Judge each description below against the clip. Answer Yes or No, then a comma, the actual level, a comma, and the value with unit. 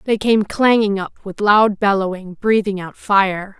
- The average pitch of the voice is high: Yes, high, 200 Hz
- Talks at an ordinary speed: Yes, average, 165 wpm